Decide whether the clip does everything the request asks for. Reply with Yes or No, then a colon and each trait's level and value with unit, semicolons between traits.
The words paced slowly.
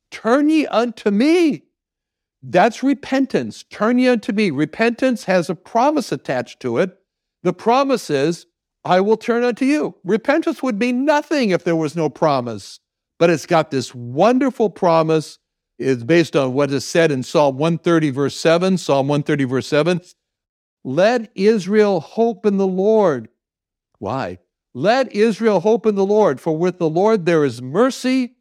No: average, 160 wpm